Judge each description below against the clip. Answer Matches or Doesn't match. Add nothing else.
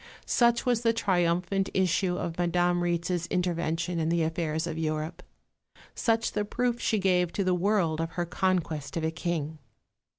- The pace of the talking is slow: Doesn't match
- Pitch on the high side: Doesn't match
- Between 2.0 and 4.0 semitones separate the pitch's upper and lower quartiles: Matches